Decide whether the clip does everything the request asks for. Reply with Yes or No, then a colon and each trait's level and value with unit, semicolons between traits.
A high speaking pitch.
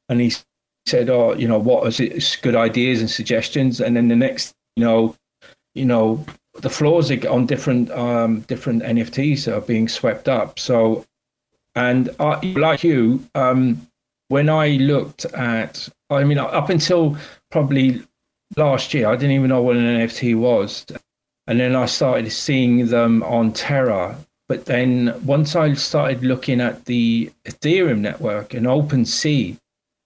No: low, 125 Hz